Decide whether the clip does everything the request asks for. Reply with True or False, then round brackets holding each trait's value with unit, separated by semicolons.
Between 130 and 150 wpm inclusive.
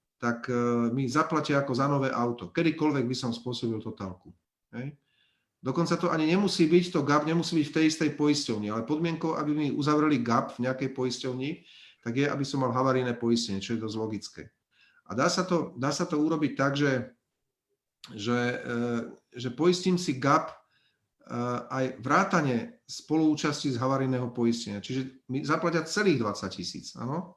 False (160 wpm)